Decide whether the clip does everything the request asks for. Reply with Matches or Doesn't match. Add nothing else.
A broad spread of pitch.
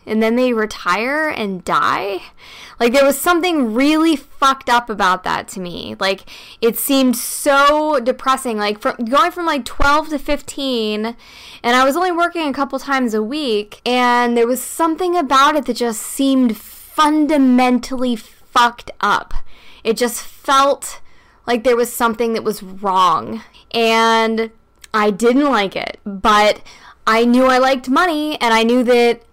Doesn't match